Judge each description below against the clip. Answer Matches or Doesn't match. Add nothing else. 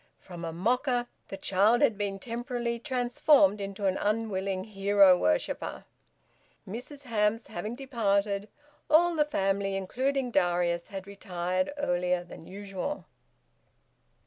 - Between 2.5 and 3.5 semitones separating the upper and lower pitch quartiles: Doesn't match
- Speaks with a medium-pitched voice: Doesn't match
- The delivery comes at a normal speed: Doesn't match